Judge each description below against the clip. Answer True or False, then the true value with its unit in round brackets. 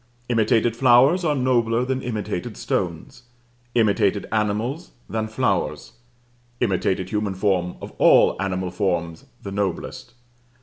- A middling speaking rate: False (115 wpm)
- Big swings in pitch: False (4.1 semitones)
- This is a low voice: True (110 Hz)